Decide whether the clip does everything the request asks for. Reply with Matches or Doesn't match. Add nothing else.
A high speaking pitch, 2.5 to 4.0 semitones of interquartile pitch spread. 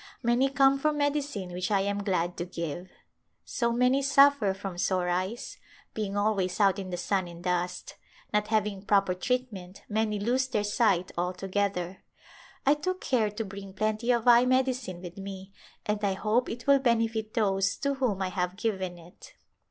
Doesn't match